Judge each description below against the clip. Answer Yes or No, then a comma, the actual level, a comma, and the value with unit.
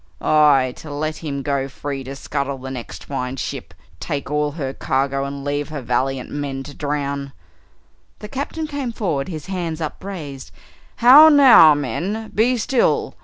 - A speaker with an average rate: Yes, average, 160 wpm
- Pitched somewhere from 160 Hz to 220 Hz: No, medium, 145 Hz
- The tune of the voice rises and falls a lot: No, average, 4.7 semitones